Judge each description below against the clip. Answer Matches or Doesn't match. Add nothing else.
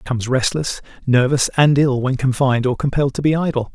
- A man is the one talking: Matches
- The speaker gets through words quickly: Matches